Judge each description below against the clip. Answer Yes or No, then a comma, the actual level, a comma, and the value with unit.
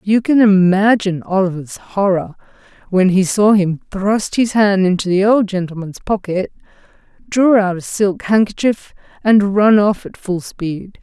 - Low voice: No, high, 195 Hz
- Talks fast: No, average, 150 wpm